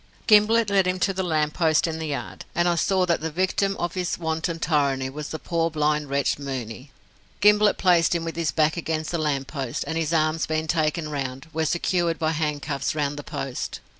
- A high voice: No, medium, 160 Hz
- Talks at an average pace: No, fast, 210 wpm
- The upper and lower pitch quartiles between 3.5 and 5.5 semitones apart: No, narrow, 2.6 semitones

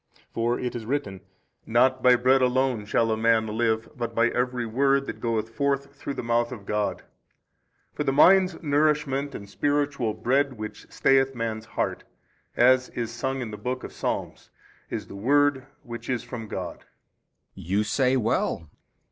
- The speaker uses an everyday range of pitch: Yes, average, 3.2 semitones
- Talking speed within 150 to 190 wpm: Yes, average, 170 wpm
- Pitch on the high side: No, low, 125 Hz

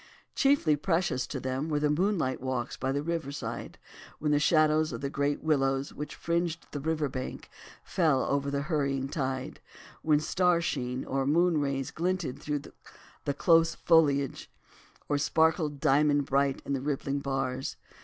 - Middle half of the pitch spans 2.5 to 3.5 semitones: Yes, average, 2.9 semitones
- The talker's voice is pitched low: No, medium, 145 Hz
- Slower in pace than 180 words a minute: Yes, average, 155 wpm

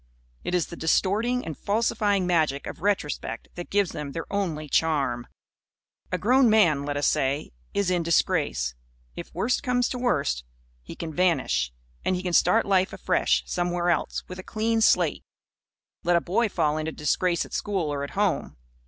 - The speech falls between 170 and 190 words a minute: Yes, average, 175 wpm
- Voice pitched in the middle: Yes, medium, 175 Hz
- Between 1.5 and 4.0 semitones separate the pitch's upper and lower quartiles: No, average, 5.1 semitones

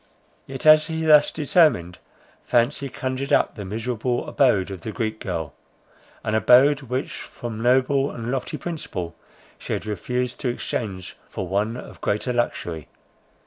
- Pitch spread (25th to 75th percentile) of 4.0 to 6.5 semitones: Yes, average, 4.3 semitones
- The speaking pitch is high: No, low, 120 Hz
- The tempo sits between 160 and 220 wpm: No, average, 145 wpm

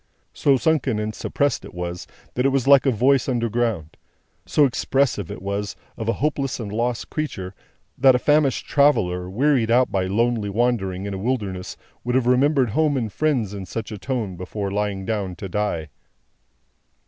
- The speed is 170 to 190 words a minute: Yes, average, 175 wpm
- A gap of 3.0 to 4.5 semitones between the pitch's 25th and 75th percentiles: No, average, 5.1 semitones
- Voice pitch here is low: Yes, low, 115 Hz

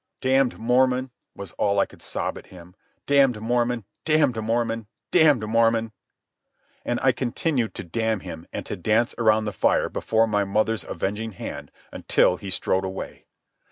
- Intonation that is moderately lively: Yes, average, 3.1 semitones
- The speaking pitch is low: Yes, low, 115 Hz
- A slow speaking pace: No, average, 155 wpm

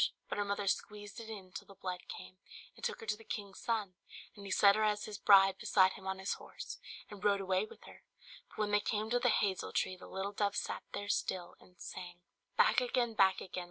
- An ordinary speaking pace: No, fast, 235 wpm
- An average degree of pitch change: No, narrow, 2.0 semitones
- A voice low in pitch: No, high, 200 Hz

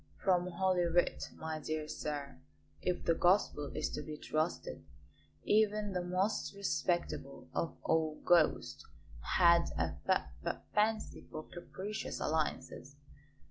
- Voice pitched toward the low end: No, medium, 170 Hz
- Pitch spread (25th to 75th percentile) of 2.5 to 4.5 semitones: Yes, average, 3.4 semitones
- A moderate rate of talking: No, slow, 125 wpm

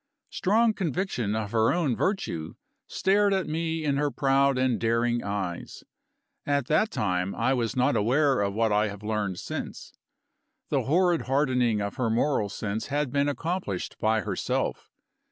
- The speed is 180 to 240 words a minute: No, average, 155 wpm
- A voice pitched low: Yes, low, 130 Hz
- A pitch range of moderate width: No, wide, 6.1 semitones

